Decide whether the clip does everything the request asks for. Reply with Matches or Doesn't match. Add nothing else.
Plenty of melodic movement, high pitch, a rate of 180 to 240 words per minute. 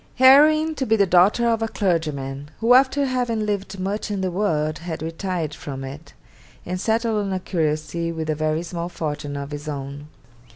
Doesn't match